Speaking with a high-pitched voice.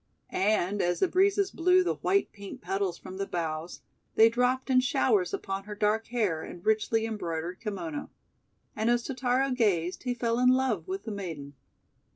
Yes: high, 215 Hz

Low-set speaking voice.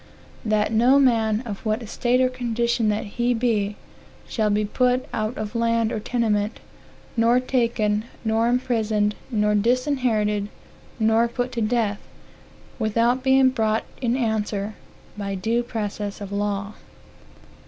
No: high, 225 Hz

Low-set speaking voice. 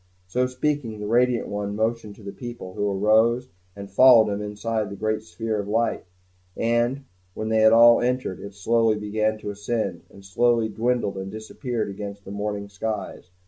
Yes: low, 110 Hz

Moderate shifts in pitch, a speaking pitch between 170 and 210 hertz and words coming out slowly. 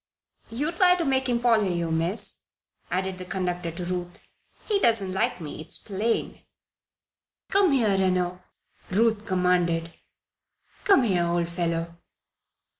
Yes: average, 4.9 semitones; medium, 185 Hz; slow, 130 wpm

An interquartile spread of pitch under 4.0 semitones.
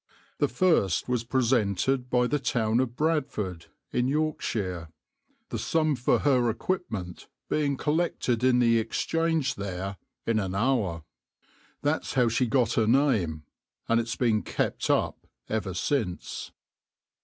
No: average, 4.7 semitones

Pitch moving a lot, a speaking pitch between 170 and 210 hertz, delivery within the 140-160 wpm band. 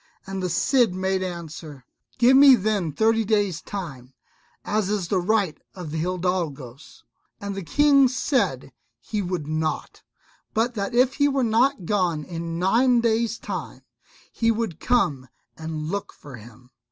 Yes: wide, 6.1 semitones; high, 190 Hz; average, 155 wpm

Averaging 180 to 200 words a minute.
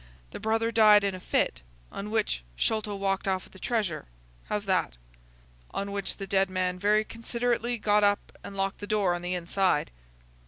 Yes: average, 185 wpm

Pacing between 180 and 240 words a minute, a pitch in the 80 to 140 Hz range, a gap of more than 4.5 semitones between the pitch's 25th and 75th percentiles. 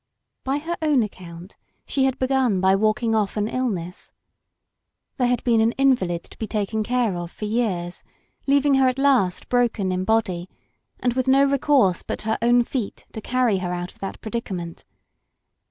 No: average, 185 wpm; high, 225 Hz; average, 5.3 semitones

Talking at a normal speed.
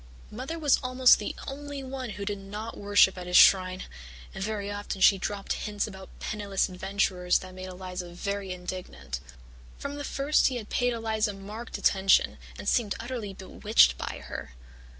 Yes: average, 170 wpm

